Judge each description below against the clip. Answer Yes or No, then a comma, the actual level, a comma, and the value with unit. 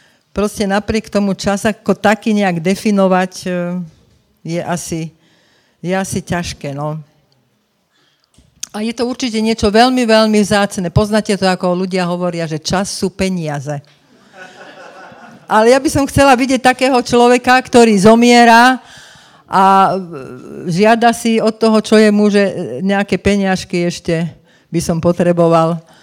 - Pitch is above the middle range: Yes, high, 195 Hz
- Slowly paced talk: No, average, 130 wpm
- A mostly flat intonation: No, average, 4.0 semitones